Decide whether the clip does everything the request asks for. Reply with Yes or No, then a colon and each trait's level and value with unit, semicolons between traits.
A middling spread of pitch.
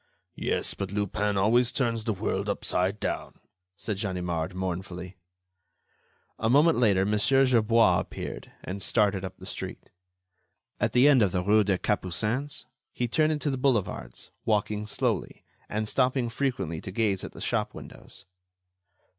Yes: average, 4.1 semitones